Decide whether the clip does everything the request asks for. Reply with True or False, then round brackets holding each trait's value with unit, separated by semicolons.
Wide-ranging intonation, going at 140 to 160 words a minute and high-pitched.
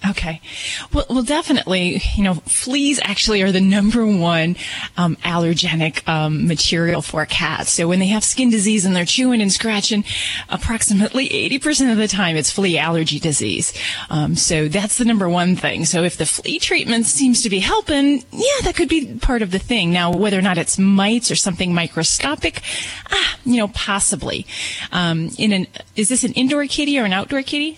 False (6.2 semitones; 190 wpm; 200 Hz)